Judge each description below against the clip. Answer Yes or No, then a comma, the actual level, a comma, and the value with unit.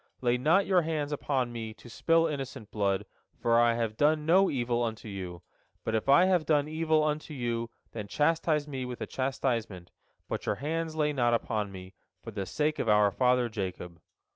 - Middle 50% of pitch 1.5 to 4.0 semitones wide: No, wide, 5.5 semitones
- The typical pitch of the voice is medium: No, low, 125 Hz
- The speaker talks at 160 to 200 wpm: Yes, average, 190 wpm